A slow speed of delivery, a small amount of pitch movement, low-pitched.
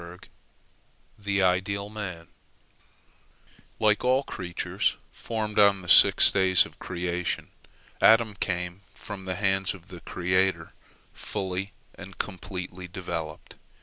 Yes: slow, 115 wpm; narrow, 2.0 semitones; very low, 95 Hz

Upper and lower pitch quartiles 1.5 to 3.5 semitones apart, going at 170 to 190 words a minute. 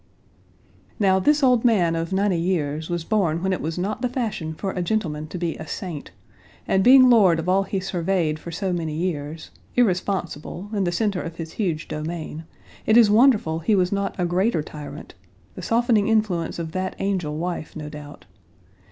No: average, 3.9 semitones; average, 185 wpm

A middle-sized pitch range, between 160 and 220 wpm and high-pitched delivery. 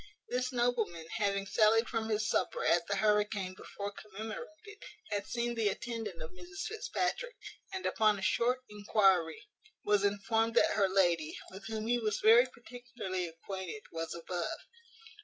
No: average, 3.6 semitones; average, 150 wpm; high, 210 Hz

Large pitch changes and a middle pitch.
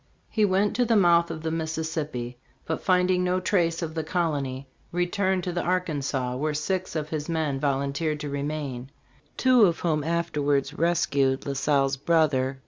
No: average, 3.9 semitones; medium, 160 Hz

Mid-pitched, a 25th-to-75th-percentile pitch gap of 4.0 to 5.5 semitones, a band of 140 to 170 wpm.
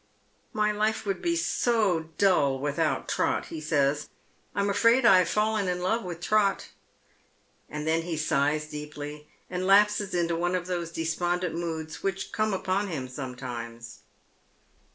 Yes: medium, 175 Hz; average, 4.9 semitones; average, 150 wpm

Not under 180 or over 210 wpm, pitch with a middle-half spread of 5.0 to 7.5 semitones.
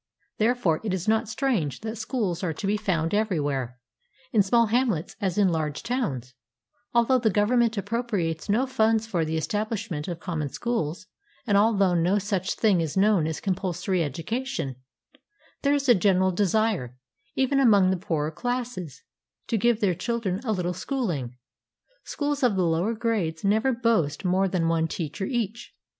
No: average, 165 wpm; wide, 5.5 semitones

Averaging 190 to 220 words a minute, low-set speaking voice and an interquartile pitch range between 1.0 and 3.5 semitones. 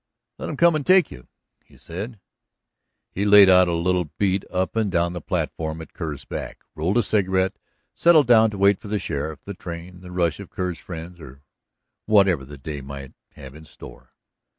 No: average, 195 wpm; very low, 90 Hz; average, 4.3 semitones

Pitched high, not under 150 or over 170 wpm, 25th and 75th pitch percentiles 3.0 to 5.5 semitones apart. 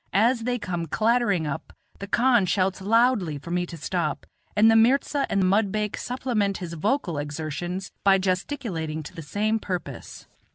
Yes: high, 195 Hz; average, 160 wpm; average, 4.9 semitones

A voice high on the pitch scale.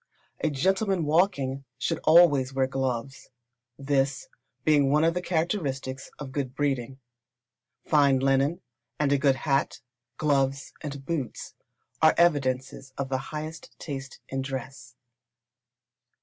No: medium, 140 Hz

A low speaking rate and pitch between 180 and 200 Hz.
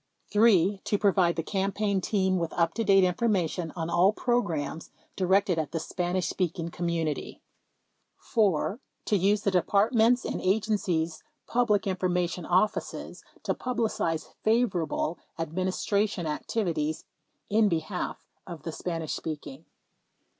Yes: slow, 130 wpm; medium, 185 Hz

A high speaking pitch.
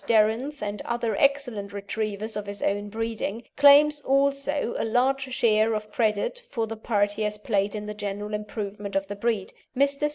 Yes: high, 220 Hz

